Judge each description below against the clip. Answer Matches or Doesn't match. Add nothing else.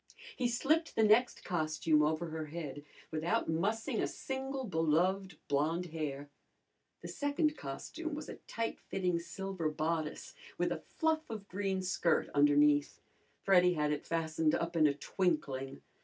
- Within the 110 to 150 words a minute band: Matches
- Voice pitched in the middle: Matches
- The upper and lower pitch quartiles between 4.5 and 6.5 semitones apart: Matches